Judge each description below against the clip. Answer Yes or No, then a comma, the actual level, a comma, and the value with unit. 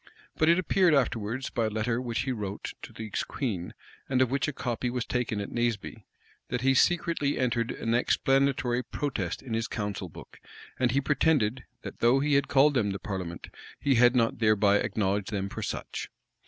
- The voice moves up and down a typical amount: Yes, average, 3.9 semitones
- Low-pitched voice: Yes, low, 120 Hz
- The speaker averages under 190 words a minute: No, average, 195 wpm